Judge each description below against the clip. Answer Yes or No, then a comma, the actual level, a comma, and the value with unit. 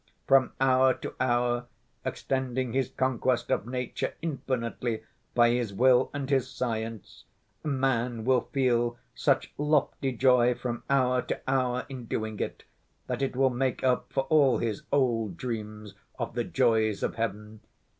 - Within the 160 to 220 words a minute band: No, average, 145 wpm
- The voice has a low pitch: Yes, low, 125 Hz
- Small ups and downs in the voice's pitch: Yes, narrow, 2.1 semitones